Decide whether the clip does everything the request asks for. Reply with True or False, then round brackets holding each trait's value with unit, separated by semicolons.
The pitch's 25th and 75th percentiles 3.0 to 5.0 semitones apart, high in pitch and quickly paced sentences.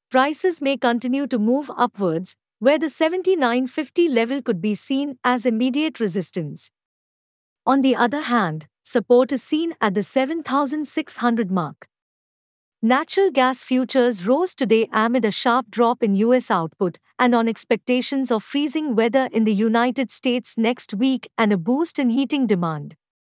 False (3.7 semitones; 245 Hz; 145 wpm)